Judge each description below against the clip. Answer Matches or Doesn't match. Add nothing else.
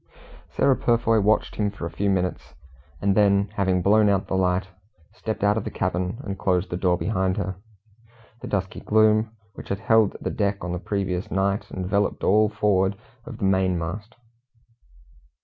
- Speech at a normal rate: Matches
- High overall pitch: Doesn't match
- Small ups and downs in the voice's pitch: Matches